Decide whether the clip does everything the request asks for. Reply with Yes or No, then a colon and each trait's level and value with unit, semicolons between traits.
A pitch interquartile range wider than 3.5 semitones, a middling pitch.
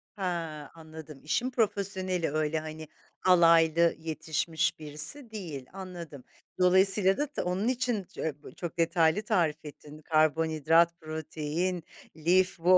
No: average, 3.0 semitones; medium, 165 Hz